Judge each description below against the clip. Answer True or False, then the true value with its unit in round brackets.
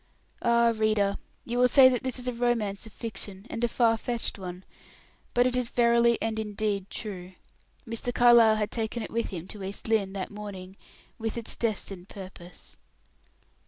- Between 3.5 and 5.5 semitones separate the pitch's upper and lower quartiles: False (3.0 semitones)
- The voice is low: False (220 Hz)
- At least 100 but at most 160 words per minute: False (175 wpm)